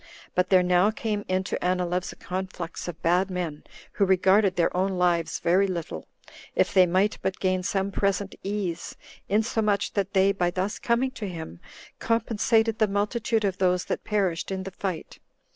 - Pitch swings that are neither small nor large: No, narrow, 2.2 semitones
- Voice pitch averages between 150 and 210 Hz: Yes, high, 190 Hz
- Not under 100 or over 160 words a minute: No, average, 175 wpm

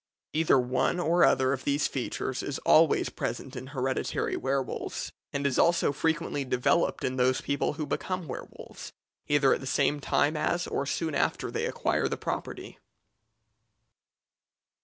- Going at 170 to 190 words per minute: No, average, 150 wpm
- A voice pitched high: No, medium, 140 Hz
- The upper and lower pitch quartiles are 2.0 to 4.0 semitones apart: Yes, average, 3.0 semitones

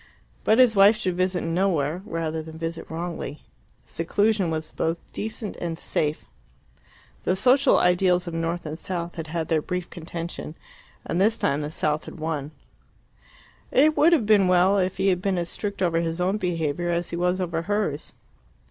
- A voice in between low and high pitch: Yes, medium, 175 Hz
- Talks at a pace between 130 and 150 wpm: No, average, 175 wpm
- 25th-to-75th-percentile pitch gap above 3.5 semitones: No, average, 2.8 semitones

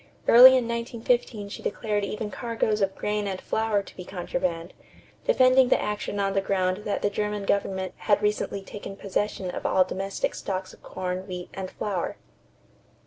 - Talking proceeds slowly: No, average, 170 wpm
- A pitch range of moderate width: No, narrow, 2.0 semitones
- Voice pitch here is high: Yes, high, 200 Hz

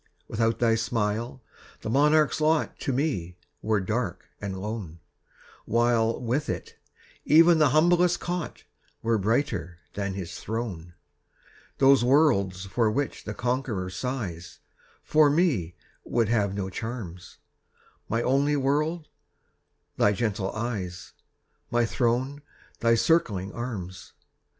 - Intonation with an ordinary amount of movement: No, wide, 5.8 semitones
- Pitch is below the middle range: Yes, low, 115 Hz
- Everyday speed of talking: No, slow, 115 wpm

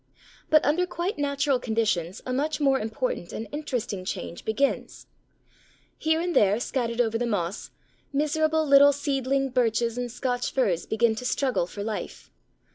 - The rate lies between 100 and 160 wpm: Yes, average, 150 wpm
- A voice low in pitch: No, very high, 250 Hz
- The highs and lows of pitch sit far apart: No, average, 4.4 semitones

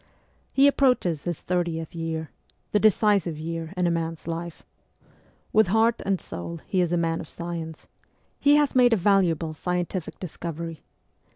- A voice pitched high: No, medium, 175 Hz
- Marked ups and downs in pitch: No, average, 3.4 semitones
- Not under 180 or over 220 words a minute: No, average, 155 wpm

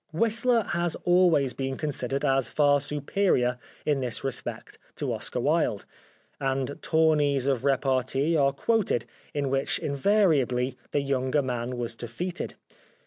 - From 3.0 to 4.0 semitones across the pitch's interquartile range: Yes, average, 3.4 semitones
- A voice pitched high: No, medium, 140 Hz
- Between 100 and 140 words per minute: Yes, slow, 135 wpm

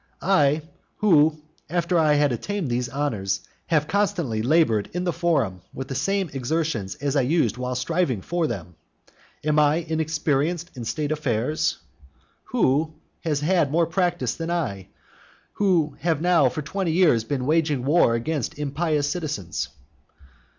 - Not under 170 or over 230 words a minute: No, average, 145 wpm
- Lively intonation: No, average, 4.8 semitones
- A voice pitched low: No, medium, 150 Hz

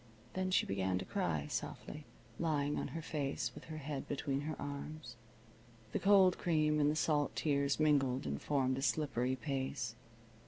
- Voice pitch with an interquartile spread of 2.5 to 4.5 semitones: Yes, average, 2.8 semitones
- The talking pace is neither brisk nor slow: Yes, average, 165 wpm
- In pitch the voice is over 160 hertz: No, medium, 145 Hz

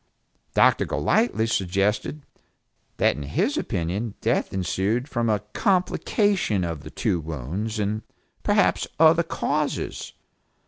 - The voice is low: Yes, low, 105 Hz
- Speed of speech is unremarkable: No, slow, 110 wpm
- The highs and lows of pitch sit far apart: Yes, wide, 8.3 semitones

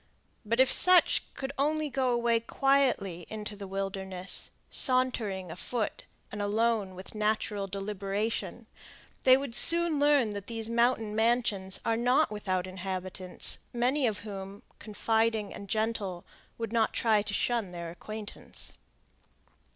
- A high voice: Yes, high, 215 Hz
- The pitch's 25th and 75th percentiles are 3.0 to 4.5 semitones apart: Yes, average, 3.5 semitones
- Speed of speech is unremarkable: No, slow, 130 wpm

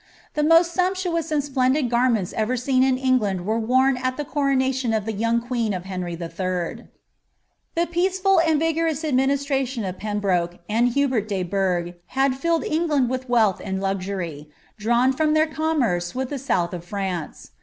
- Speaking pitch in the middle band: No, very high, 255 Hz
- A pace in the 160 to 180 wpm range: Yes, average, 165 wpm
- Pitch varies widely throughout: Yes, wide, 6.6 semitones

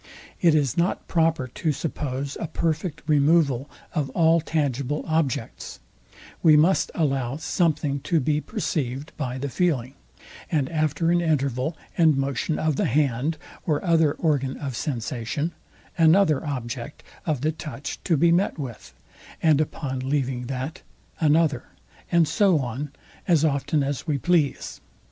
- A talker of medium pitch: Yes, medium, 150 Hz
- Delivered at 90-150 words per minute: Yes, average, 140 wpm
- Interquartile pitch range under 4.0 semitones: Yes, average, 3.3 semitones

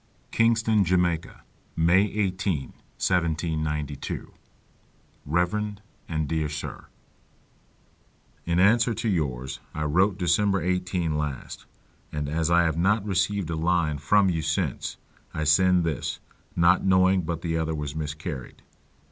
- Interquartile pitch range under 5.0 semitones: Yes, average, 3.4 semitones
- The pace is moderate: No, slow, 120 wpm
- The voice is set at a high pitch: No, very low, 85 Hz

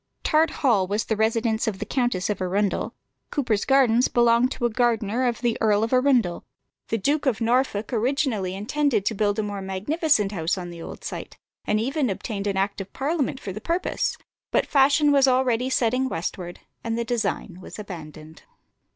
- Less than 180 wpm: No, average, 185 wpm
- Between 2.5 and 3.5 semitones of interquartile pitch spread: No, average, 4.4 semitones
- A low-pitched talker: No, high, 225 Hz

